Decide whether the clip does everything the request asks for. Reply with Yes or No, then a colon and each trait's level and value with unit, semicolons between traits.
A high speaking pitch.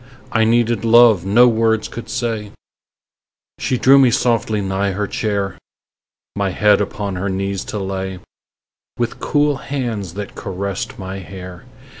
No: low, 105 Hz